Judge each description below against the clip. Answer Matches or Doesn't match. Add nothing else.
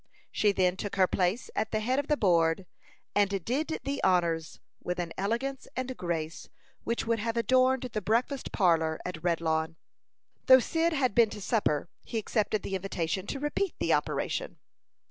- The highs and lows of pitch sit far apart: Matches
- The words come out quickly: Doesn't match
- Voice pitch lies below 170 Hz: Doesn't match